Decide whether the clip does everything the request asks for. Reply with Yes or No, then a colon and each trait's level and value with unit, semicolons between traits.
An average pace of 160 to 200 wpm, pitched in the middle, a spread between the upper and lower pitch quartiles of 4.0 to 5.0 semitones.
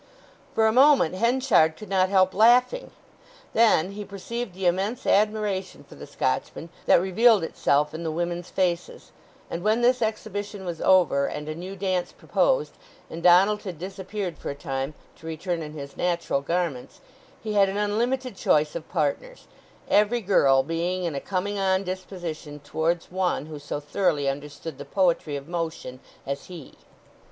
Yes: average, 165 wpm; medium, 180 Hz; average, 4.5 semitones